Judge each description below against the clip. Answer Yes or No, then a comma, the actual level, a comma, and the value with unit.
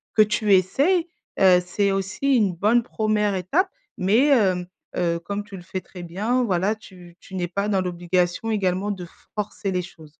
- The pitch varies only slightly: No, average, 3.0 semitones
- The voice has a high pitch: Yes, high, 195 Hz